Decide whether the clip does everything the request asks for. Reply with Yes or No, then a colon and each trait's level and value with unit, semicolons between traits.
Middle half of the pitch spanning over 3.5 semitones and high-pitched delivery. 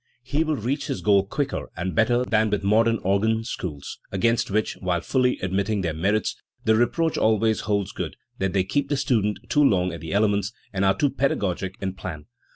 No: average, 4.0 semitones; low, 105 Hz